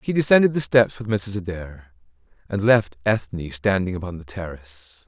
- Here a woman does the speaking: No, male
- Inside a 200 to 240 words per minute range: No, average, 165 wpm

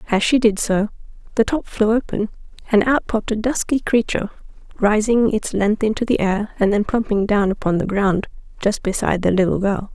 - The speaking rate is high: No, average, 195 wpm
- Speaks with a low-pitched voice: No, high, 210 Hz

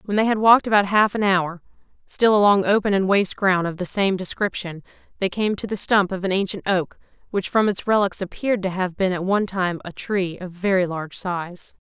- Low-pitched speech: No, high, 190 Hz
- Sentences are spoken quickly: Yes, fast, 220 wpm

